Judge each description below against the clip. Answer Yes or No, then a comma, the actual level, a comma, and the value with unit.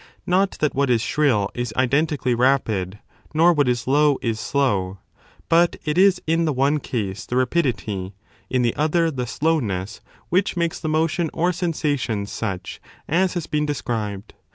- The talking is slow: No, average, 160 wpm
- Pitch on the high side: No, medium, 140 Hz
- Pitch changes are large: Yes, wide, 6.2 semitones